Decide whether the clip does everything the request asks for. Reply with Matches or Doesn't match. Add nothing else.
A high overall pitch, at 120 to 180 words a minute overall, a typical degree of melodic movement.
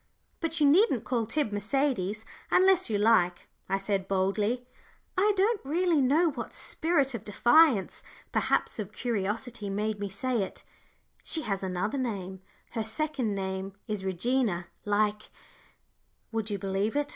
Doesn't match